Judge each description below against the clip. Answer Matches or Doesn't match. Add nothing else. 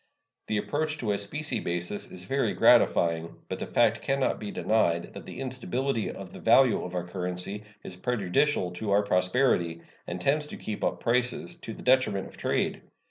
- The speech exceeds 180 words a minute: Matches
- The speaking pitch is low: Matches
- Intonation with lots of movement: Matches